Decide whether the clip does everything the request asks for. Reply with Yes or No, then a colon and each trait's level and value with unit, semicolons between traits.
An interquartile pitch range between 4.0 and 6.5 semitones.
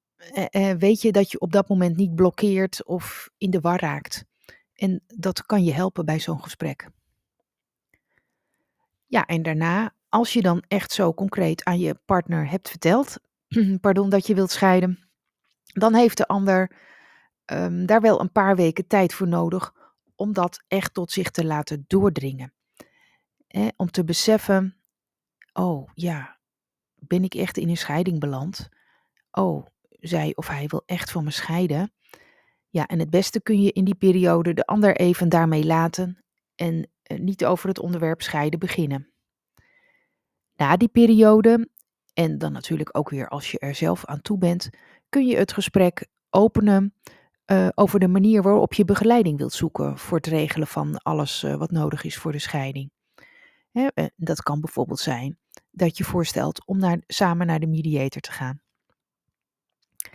No: average, 3.4 semitones